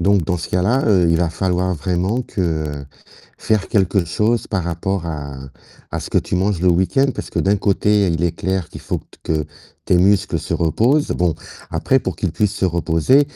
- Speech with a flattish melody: No, average, 3.3 semitones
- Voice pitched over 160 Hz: No, very low, 90 Hz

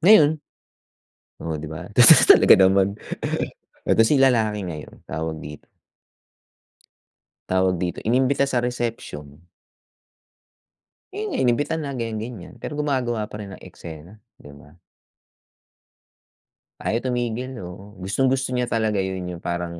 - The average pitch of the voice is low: Yes, low, 110 Hz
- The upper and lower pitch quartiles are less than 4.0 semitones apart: No, wide, 6.1 semitones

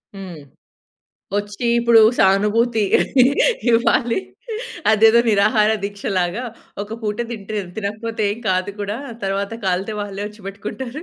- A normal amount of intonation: No, narrow, 2.2 semitones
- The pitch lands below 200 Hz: No, high, 210 Hz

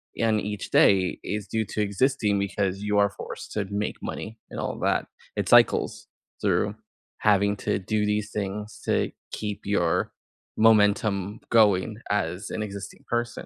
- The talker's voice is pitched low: Yes, low, 105 Hz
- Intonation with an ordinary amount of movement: No, narrow, 1.3 semitones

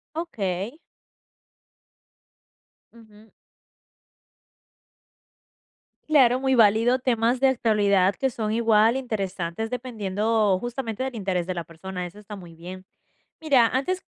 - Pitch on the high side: Yes, high, 220 Hz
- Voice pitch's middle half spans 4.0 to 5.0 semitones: Yes, average, 4.5 semitones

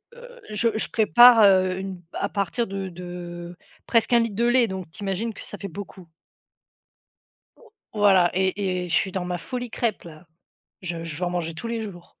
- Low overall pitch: No, high, 190 Hz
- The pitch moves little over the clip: No, average, 4.0 semitones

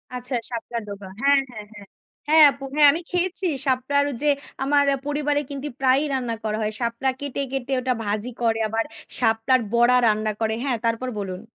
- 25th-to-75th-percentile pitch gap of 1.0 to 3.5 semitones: No, average, 4.0 semitones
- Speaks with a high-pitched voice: Yes, very high, 250 Hz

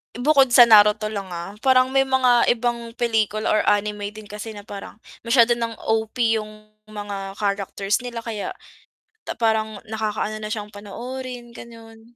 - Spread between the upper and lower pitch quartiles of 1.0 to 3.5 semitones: Yes, narrow, 2.4 semitones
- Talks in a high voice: Yes, high, 220 Hz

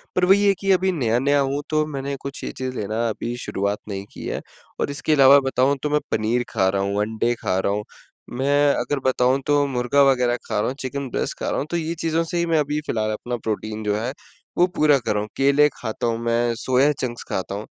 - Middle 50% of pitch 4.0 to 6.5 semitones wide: Yes, average, 4.5 semitones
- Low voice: Yes, low, 130 Hz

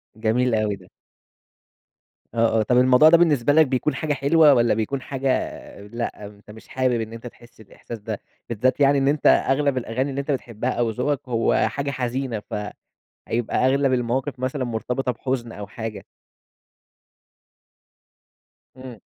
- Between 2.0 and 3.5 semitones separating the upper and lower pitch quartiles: Yes, average, 3.2 semitones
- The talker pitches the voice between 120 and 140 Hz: Yes, low, 125 Hz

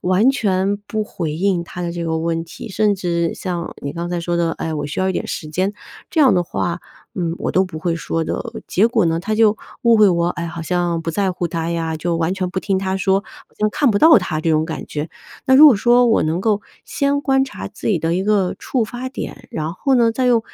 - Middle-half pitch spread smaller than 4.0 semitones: No, average, 4.3 semitones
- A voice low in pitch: No, medium, 185 Hz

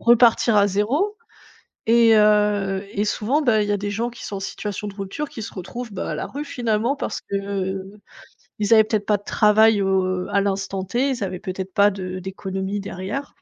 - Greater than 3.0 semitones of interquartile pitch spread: No, narrow, 2.5 semitones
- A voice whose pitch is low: No, high, 205 Hz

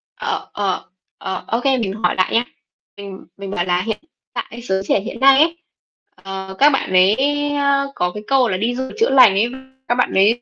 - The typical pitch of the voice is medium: No, high, 220 Hz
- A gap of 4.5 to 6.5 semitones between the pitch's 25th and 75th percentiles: Yes, average, 5.2 semitones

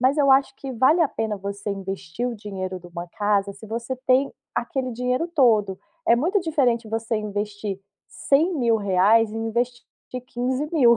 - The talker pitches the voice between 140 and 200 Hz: No, high, 230 Hz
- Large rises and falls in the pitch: No, average, 4.2 semitones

